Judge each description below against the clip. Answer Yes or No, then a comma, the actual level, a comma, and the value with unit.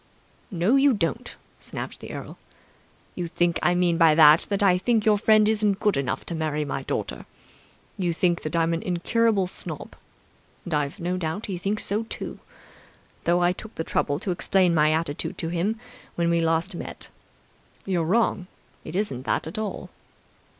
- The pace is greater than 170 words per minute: Yes, average, 180 wpm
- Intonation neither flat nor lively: Yes, average, 3.8 semitones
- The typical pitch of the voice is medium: Yes, medium, 175 Hz